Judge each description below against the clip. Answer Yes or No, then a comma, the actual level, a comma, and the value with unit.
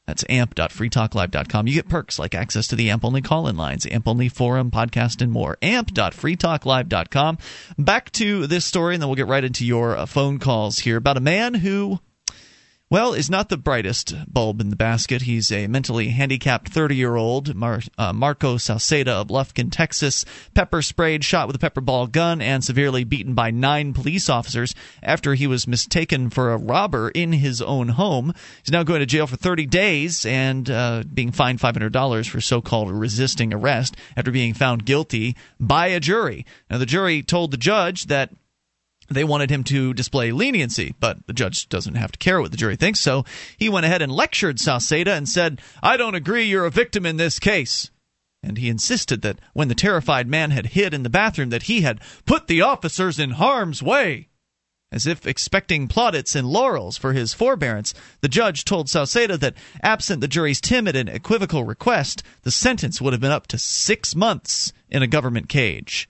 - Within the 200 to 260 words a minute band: No, average, 190 wpm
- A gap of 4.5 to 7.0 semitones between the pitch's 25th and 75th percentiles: Yes, wide, 5.6 semitones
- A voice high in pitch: No, low, 135 Hz